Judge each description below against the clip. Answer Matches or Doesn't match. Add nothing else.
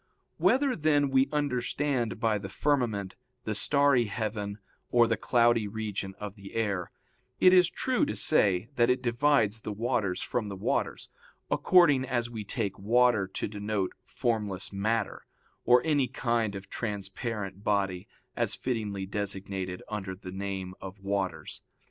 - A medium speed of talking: Matches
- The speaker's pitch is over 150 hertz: Doesn't match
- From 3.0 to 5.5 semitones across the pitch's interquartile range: Matches